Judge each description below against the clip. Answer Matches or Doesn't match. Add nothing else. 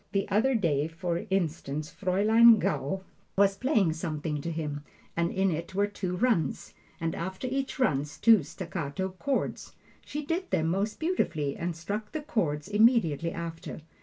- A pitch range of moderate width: Matches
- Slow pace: Doesn't match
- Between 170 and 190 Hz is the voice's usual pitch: Matches